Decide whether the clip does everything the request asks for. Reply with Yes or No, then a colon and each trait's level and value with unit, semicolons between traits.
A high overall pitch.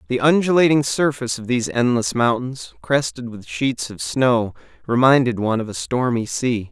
No: low, 125 Hz